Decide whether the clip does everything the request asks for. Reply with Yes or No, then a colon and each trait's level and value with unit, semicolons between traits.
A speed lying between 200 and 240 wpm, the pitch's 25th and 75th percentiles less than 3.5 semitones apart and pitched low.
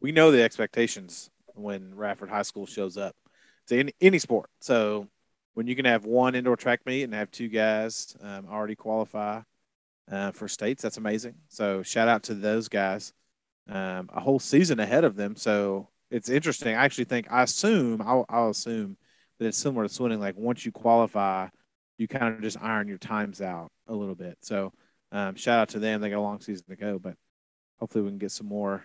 Yes: fast, 205 wpm; average, 2.8 semitones; low, 110 Hz